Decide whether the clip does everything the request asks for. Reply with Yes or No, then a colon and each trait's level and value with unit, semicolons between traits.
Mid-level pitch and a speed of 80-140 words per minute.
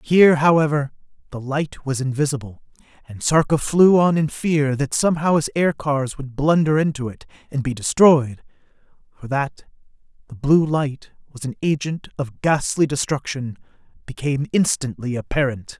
Yes: medium, 145 Hz; slow, 135 wpm